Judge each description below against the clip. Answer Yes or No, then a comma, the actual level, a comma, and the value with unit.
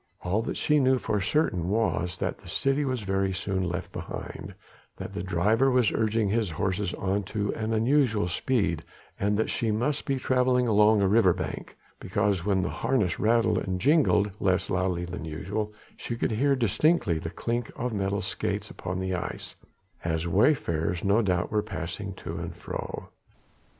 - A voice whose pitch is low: Yes, low, 105 Hz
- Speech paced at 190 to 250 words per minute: No, average, 170 wpm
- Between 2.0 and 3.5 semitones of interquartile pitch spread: No, average, 4.2 semitones